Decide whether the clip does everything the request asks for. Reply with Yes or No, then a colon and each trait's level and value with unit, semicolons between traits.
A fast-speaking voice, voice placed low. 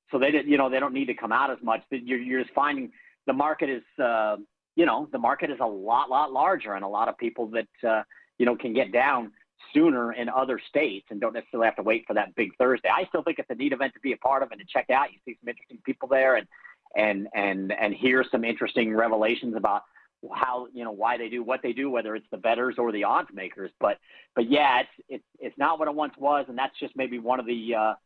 Yes: fast, 265 wpm; low, 120 Hz